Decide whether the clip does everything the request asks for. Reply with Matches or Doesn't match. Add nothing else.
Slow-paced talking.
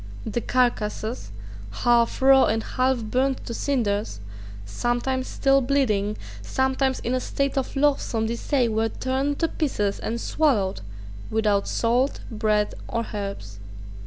Matches